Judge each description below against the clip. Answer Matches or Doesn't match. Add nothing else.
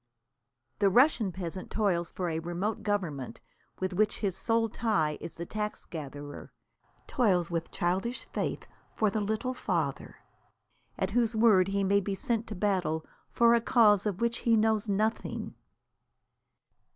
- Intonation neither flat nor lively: Matches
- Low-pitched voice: Doesn't match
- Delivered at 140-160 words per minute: Matches